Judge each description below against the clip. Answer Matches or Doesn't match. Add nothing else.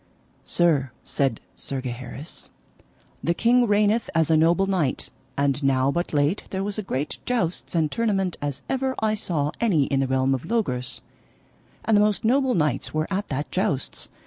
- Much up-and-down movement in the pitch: Matches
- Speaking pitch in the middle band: Matches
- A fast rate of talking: Doesn't match